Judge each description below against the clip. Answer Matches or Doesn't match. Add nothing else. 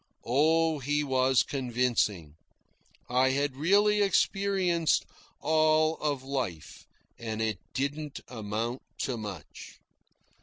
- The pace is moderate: Doesn't match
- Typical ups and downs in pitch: Matches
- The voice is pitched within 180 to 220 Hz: Doesn't match